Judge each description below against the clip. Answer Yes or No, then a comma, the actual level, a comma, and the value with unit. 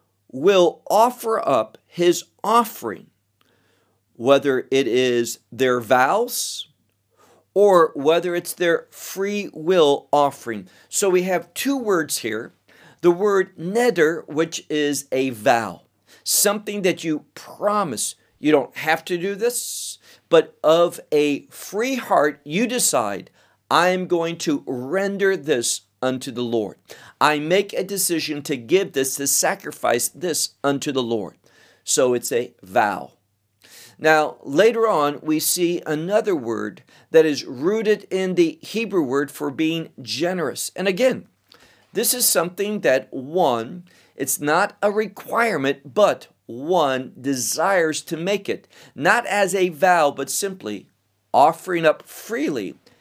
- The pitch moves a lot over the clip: Yes, wide, 6.4 semitones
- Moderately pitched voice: Yes, medium, 165 Hz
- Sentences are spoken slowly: Yes, slow, 130 wpm